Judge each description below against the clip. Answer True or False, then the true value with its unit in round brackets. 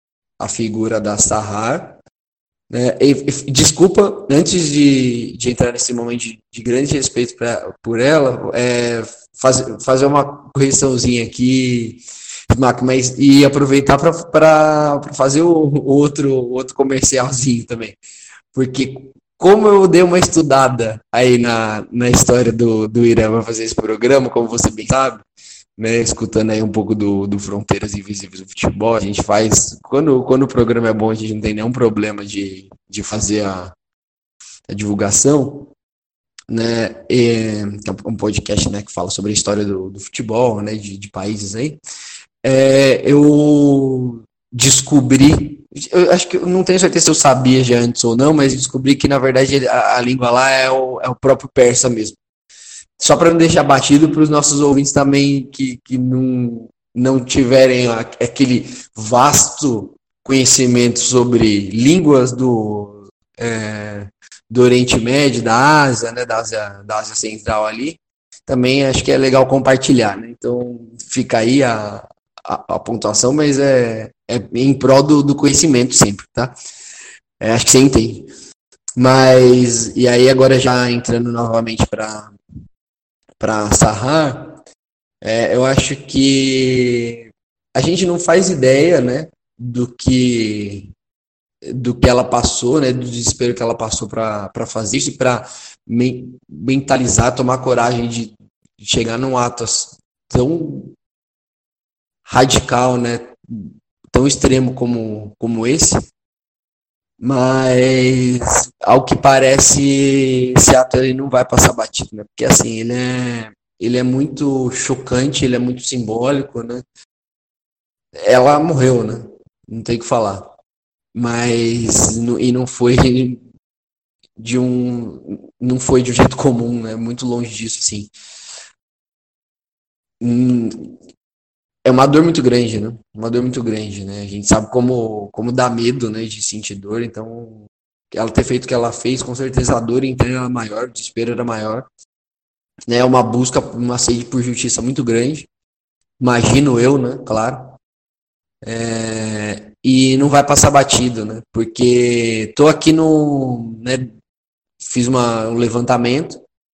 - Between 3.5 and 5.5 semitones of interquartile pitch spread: False (2.8 semitones)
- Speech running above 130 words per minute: True (145 wpm)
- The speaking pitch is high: False (125 Hz)